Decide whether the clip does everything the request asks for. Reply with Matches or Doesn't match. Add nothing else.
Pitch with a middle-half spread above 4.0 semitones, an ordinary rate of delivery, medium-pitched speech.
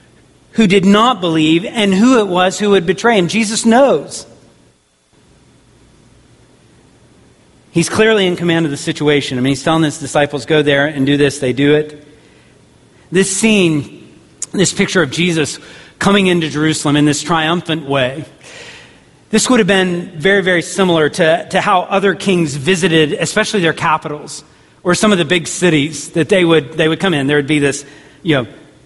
Matches